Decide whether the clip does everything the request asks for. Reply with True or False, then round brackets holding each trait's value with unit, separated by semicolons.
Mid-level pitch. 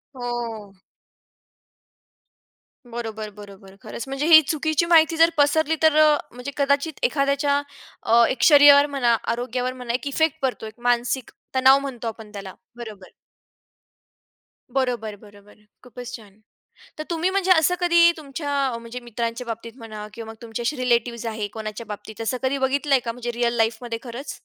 False (245 Hz)